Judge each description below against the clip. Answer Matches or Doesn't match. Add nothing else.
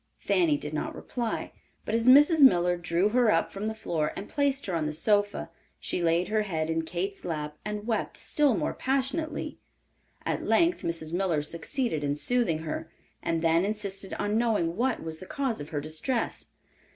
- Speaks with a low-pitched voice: Doesn't match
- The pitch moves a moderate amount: Doesn't match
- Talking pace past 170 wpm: Matches